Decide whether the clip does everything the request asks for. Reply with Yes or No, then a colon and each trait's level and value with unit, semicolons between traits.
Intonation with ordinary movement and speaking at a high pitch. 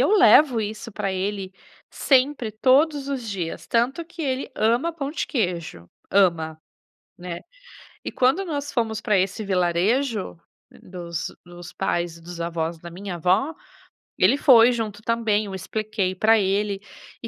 No: wide, 5.9 semitones; high, 210 Hz